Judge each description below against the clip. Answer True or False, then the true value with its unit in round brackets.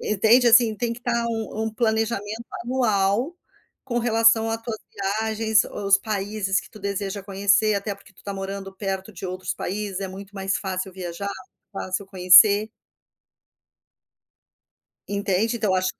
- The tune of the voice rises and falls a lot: False (2.5 semitones)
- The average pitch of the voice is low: False (205 Hz)